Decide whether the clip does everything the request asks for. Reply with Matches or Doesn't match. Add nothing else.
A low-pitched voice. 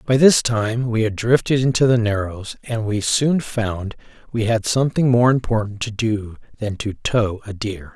Matches